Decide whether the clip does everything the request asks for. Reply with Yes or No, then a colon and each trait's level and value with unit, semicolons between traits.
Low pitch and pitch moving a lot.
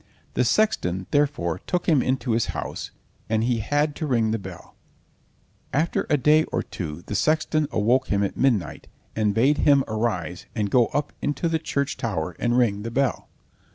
Yes: low, 120 Hz; wide, 5.9 semitones